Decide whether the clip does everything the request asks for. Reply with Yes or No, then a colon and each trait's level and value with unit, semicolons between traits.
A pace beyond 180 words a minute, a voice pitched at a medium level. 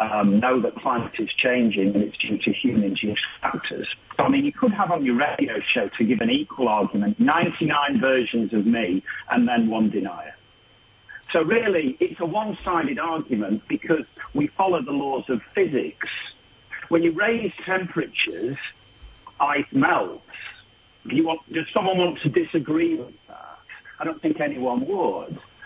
No: average, 155 wpm; medium, 170 Hz